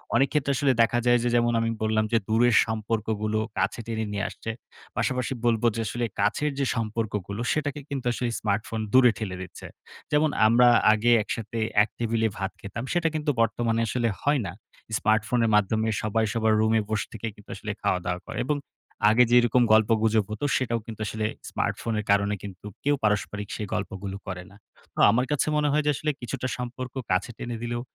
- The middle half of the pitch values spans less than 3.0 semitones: Yes, narrow, 2.4 semitones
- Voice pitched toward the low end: Yes, low, 115 Hz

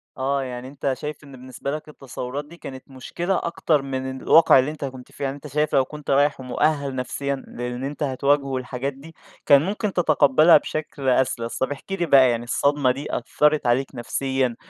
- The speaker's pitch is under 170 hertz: Yes, medium, 140 Hz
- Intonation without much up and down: Yes, narrow, 2.3 semitones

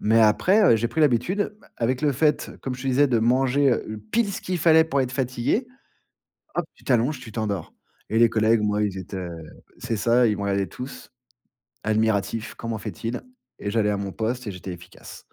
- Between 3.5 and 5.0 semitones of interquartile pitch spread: Yes, average, 4.0 semitones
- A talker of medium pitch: No, low, 115 Hz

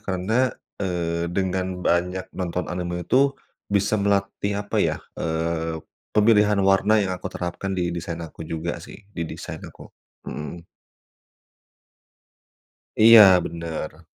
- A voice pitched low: Yes, very low, 90 Hz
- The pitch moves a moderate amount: Yes, average, 3.0 semitones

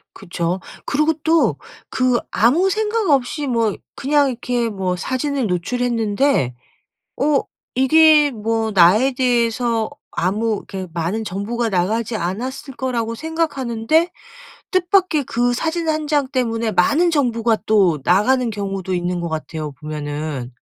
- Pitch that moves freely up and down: Yes, wide, 6.5 semitones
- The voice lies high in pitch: Yes, high, 235 Hz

